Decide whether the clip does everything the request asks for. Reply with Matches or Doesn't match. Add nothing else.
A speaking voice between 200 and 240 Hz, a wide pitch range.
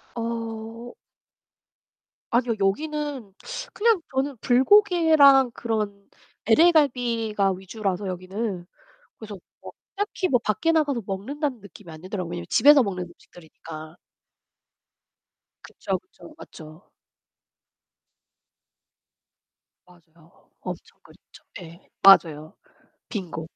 Matches